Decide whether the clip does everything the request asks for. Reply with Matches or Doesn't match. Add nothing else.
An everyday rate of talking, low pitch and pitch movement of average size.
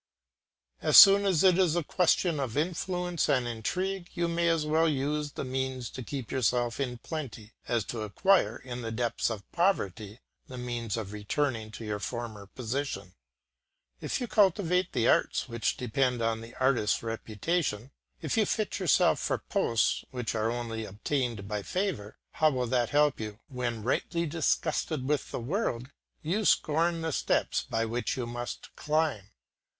Doesn't match